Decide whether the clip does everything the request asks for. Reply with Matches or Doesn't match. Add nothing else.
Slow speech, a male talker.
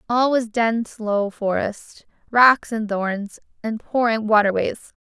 Doesn't match